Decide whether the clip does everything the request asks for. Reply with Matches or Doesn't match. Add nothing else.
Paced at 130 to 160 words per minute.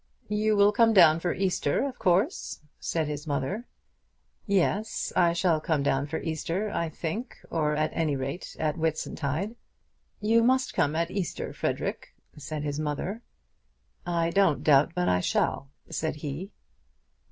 Matches